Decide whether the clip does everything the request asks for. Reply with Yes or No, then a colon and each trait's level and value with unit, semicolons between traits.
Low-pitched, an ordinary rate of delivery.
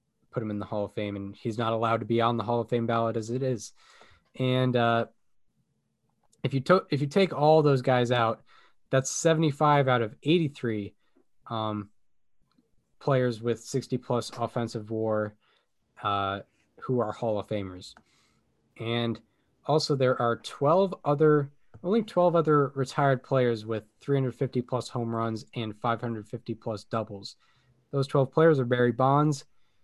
Yes: low, 120 Hz; average, 155 wpm